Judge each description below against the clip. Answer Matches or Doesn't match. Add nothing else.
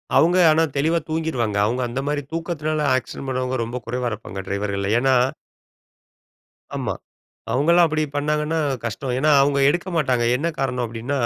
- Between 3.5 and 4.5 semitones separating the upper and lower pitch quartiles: Matches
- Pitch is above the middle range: Doesn't match